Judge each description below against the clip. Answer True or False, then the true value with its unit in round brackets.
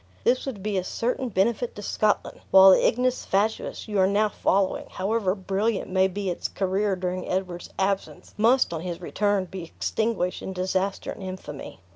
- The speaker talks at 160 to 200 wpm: True (175 wpm)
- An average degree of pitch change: False (2.3 semitones)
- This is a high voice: True (195 Hz)